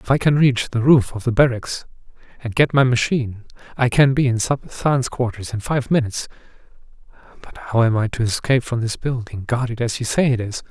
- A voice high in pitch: No, low, 120 Hz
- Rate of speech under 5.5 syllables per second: No, 5.6 syllables/s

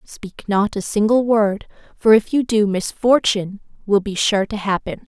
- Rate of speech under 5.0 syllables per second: Yes, 4.5 syllables/s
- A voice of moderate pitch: No, high, 210 Hz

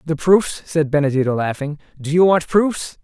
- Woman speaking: No, male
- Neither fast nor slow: Yes, average, 180 wpm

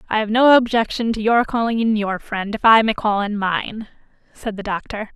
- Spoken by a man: No, female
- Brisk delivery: Yes, fast, 220 wpm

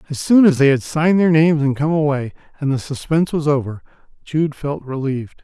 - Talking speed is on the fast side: Yes, fast, 210 wpm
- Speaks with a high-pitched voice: No, medium, 145 Hz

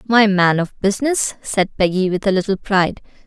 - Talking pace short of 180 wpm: No, average, 185 wpm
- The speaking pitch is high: Yes, high, 200 Hz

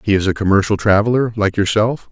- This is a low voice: Yes, low, 105 Hz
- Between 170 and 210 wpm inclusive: Yes, average, 200 wpm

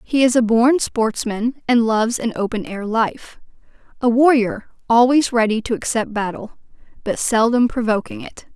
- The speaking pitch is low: No, high, 230 Hz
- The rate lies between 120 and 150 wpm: Yes, average, 145 wpm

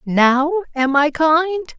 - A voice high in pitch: Yes, very high, 305 Hz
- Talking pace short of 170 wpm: Yes, slow, 135 wpm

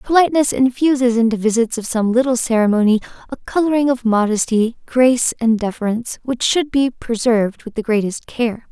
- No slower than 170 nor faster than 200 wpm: No, average, 160 wpm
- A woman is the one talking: Yes, female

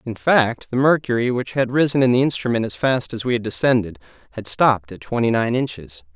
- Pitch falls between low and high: No, low, 120 Hz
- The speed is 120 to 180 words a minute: No, fast, 205 wpm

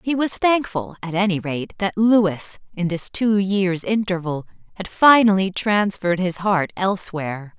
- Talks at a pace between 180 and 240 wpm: No, average, 150 wpm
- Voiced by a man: No, female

